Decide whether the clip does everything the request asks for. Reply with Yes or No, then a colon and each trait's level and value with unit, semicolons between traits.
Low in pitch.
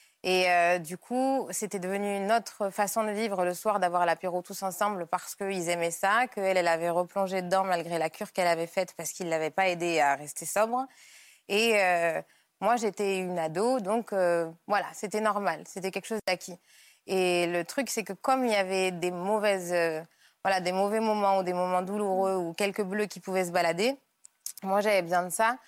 No: high, 190 Hz